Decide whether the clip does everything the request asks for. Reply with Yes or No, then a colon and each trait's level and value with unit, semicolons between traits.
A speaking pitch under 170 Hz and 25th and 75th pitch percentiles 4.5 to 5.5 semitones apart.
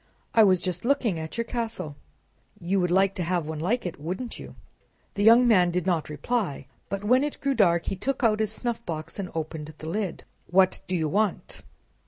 No: high, 190 Hz; average, 5.1 semitones